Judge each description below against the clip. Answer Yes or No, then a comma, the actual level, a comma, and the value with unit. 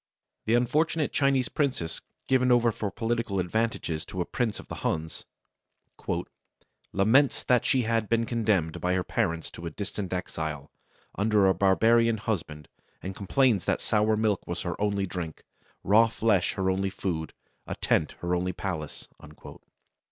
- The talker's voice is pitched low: Yes, low, 100 Hz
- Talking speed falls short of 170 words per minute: Yes, average, 150 wpm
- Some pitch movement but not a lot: Yes, average, 4.4 semitones